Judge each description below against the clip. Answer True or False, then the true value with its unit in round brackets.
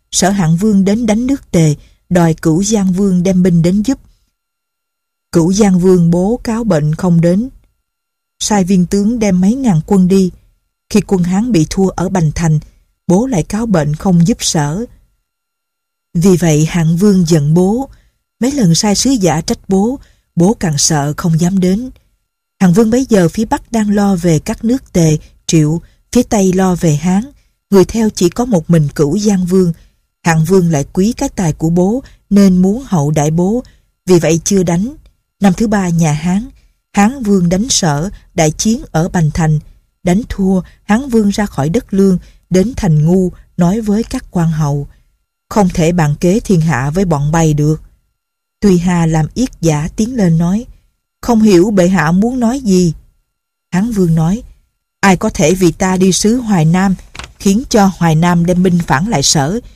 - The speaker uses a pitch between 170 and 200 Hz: True (185 Hz)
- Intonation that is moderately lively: True (4.4 semitones)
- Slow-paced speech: False (185 wpm)